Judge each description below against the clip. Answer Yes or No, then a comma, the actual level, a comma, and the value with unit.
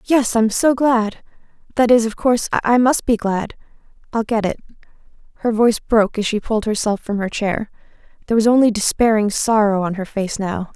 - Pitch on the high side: Yes, high, 220 Hz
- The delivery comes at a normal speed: Yes, average, 185 wpm